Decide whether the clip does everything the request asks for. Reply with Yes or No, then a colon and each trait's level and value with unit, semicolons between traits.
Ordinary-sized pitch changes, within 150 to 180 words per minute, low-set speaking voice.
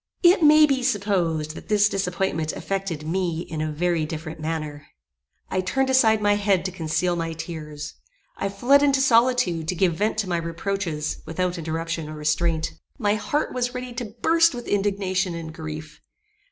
No: average, 5.0 semitones; average, 170 wpm; medium, 180 Hz